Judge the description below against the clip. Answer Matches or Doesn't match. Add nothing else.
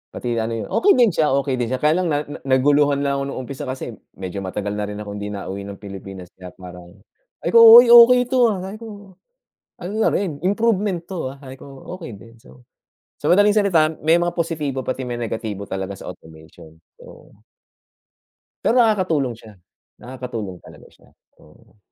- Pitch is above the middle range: Doesn't match